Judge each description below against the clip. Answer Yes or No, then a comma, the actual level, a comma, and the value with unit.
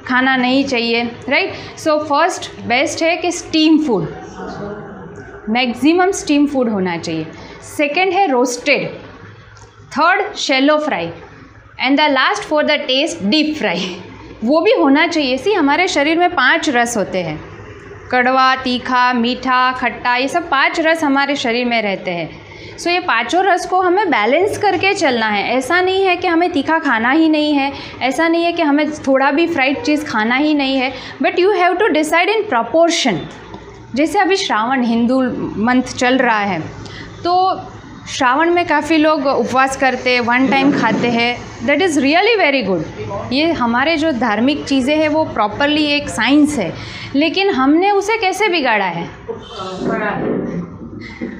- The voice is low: No, very high, 280 Hz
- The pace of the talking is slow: No, average, 160 wpm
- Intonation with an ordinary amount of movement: Yes, average, 5.0 semitones